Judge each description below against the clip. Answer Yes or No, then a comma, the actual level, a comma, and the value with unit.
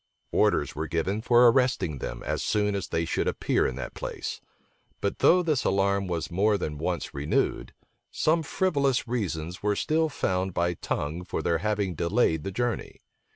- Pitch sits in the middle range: No, low, 100 Hz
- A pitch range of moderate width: No, wide, 6.2 semitones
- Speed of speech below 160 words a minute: No, average, 170 wpm